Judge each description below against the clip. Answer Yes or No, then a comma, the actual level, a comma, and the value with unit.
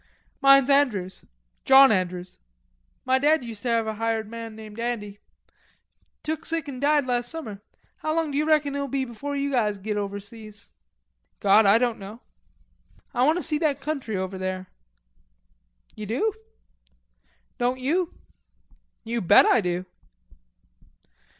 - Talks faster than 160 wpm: No, average, 140 wpm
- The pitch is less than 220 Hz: No, high, 240 Hz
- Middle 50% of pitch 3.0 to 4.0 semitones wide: No, average, 5.3 semitones